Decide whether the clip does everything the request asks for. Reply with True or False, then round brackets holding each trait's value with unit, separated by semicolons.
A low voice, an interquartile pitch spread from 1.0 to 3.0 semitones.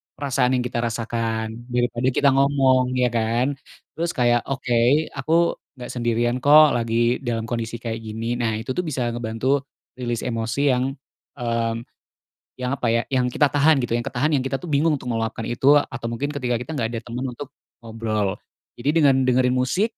True (120 Hz; 2.7 semitones)